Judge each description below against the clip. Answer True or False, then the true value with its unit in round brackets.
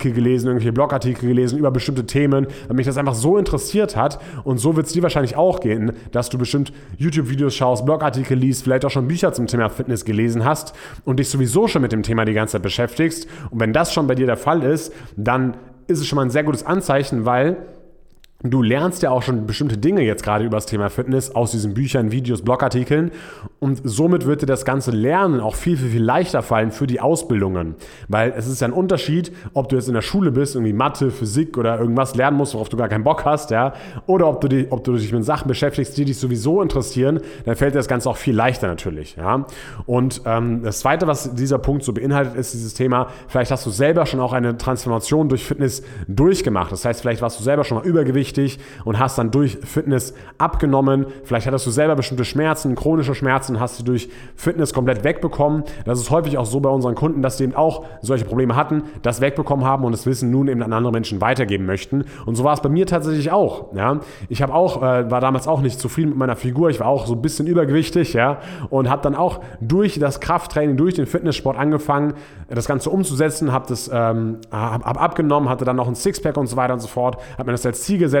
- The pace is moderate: False (230 wpm)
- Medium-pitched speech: False (130 Hz)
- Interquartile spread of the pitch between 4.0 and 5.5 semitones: False (3.4 semitones)